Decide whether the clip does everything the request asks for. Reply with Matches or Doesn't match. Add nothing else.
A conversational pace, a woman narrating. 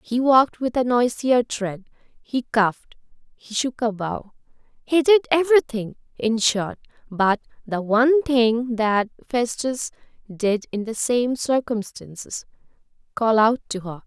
Doesn't match